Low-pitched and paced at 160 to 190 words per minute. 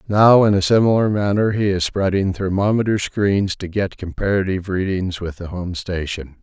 Yes: very low, 95 Hz; average, 170 wpm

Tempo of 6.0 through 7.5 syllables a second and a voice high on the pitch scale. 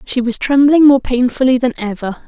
No: 5.3 syllables/s; very high, 255 Hz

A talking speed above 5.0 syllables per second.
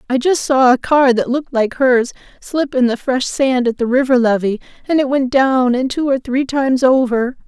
No: 4.9 syllables/s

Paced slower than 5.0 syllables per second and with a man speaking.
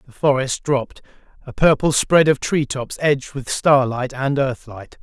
Yes: 4.5 syllables/s; male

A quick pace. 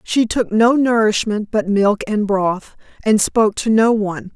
No: average, 180 wpm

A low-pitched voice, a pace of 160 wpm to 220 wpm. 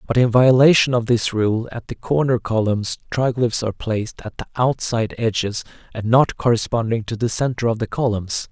Yes: low, 115 Hz; average, 185 wpm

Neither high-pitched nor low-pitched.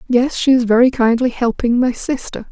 No: high, 245 Hz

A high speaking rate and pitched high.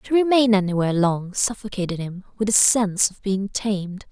No: average, 175 wpm; high, 200 Hz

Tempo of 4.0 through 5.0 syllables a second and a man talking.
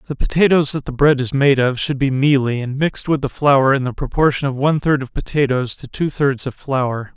No: 5.5 syllables/s; male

